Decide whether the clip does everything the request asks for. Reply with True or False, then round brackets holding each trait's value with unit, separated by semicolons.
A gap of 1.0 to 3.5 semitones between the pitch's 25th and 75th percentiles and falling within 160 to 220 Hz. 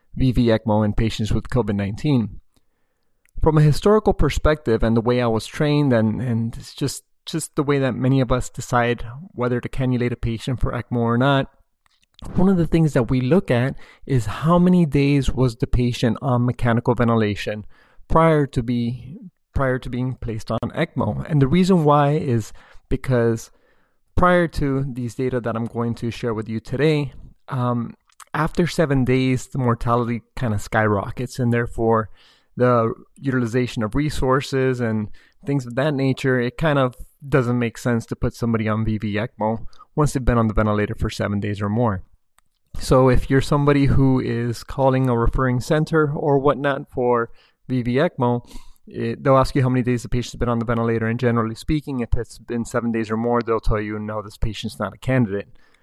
False (3.0 semitones; 125 Hz)